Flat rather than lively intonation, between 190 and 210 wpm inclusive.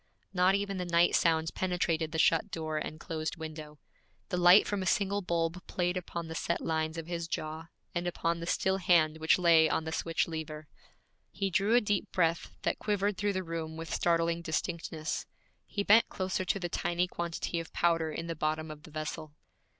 Yes: narrow, 2.3 semitones; average, 195 wpm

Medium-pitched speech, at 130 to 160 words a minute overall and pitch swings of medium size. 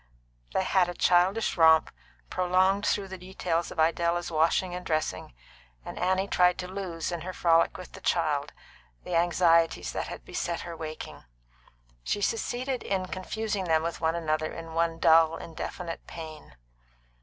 No: medium, 175 Hz; average, 155 wpm; narrow, 2.2 semitones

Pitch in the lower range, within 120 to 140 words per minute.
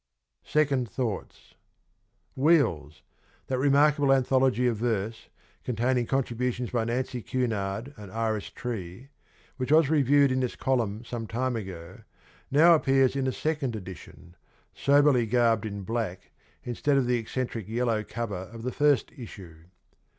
Yes: low, 120 Hz; slow, 135 wpm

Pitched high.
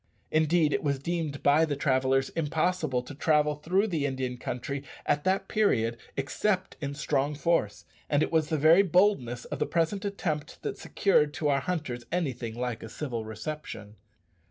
No: medium, 150 Hz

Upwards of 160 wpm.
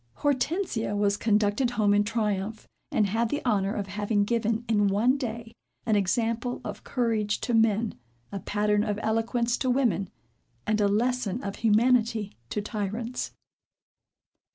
No: average, 145 wpm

